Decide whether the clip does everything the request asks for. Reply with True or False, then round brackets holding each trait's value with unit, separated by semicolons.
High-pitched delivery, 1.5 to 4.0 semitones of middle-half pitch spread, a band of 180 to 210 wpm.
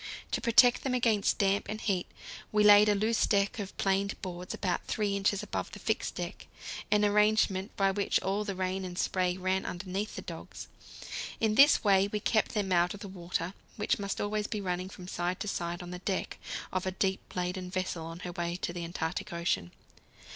True (195 Hz; 2.5 semitones; 205 wpm)